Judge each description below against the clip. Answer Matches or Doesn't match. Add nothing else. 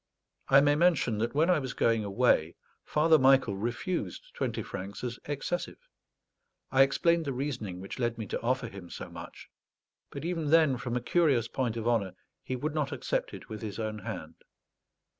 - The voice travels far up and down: Doesn't match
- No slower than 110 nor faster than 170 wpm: Doesn't match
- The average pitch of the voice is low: Matches